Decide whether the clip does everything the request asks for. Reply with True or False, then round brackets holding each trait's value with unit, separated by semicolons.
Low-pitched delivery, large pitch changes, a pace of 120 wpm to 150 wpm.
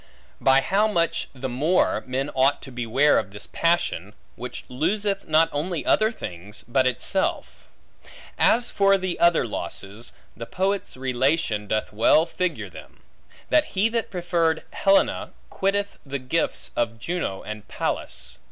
False (145 Hz; 7.5 semitones; 145 wpm)